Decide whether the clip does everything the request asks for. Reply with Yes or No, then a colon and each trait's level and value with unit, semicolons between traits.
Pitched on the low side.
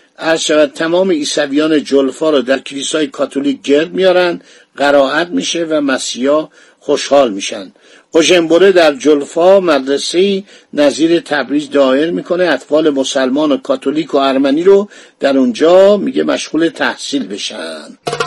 No: medium, 155 Hz